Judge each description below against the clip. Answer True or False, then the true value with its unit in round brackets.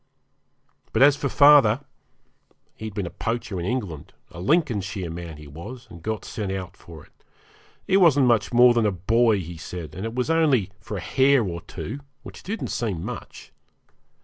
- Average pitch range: False (6.0 semitones)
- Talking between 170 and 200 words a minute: True (180 wpm)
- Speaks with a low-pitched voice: True (110 Hz)